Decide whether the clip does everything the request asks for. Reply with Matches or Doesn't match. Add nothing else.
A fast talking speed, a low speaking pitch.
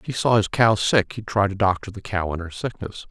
Matches